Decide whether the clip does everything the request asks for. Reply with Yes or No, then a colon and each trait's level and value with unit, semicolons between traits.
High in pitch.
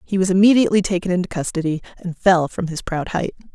No: medium, 180 Hz